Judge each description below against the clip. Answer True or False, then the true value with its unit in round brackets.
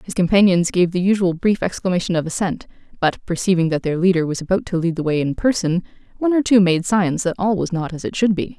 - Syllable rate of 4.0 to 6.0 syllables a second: False (6.2 syllables/s)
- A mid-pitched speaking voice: True (180 Hz)